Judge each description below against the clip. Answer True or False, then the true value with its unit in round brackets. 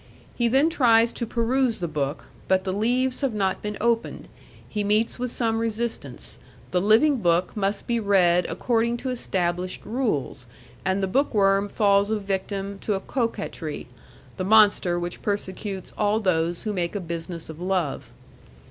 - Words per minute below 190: True (165 wpm)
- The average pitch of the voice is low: False (205 Hz)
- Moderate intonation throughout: True (3.8 semitones)